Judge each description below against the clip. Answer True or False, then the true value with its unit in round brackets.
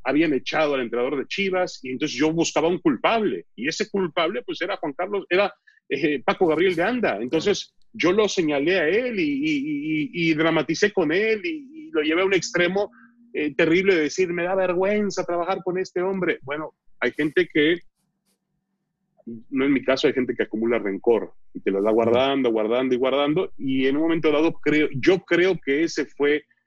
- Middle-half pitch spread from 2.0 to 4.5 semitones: False (5.1 semitones)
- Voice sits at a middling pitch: True (175 Hz)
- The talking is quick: True (200 wpm)